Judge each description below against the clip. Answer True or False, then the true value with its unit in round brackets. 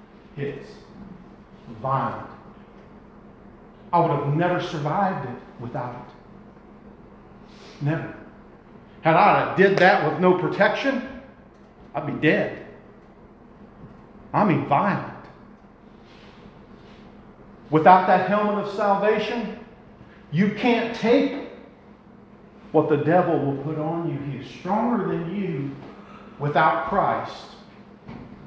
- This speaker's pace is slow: True (95 wpm)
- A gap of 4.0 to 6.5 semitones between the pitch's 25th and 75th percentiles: True (5.3 semitones)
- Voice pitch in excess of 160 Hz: True (190 Hz)